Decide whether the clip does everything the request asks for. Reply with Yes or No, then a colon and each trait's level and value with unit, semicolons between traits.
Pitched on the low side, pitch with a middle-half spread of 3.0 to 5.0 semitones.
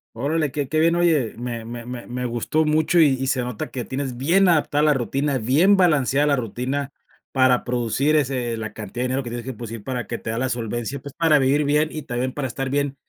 Yes: low, 130 Hz; average, 3.4 semitones